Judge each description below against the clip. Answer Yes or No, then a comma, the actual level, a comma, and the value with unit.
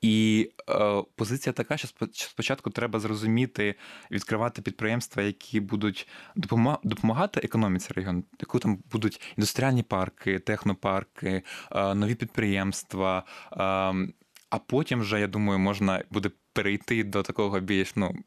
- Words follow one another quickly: No, average, 125 wpm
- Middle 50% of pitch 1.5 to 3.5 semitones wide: Yes, average, 3.1 semitones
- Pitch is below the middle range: Yes, low, 105 Hz